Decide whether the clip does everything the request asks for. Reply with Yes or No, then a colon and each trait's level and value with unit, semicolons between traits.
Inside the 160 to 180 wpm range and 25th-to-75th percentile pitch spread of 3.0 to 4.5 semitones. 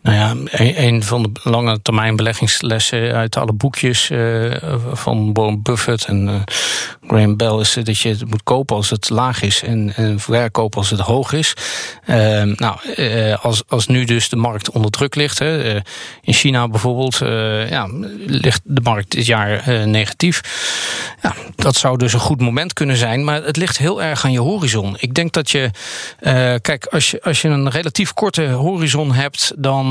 Yes: average, 170 wpm; average, 4.0 semitones